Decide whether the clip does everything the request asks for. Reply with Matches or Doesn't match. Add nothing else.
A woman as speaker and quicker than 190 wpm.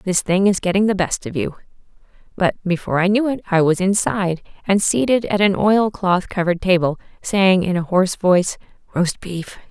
Doesn't match